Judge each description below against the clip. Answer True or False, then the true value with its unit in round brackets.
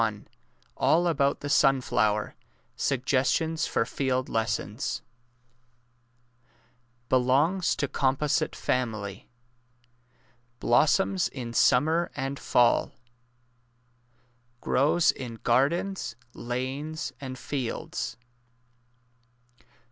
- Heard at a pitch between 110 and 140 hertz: True (135 Hz)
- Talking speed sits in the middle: False (70 wpm)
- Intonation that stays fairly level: False (4.1 semitones)